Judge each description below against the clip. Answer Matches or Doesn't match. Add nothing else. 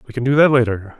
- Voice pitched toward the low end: Matches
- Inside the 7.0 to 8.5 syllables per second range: Matches